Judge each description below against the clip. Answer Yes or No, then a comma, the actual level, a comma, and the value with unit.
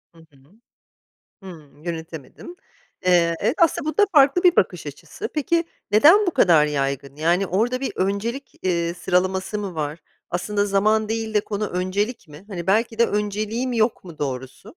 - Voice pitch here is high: Yes, high, 200 Hz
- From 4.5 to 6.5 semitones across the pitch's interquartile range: Yes, wide, 5.4 semitones